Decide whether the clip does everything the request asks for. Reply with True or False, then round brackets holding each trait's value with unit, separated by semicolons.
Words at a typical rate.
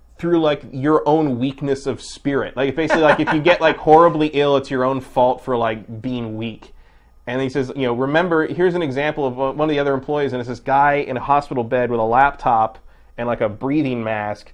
False (225 wpm)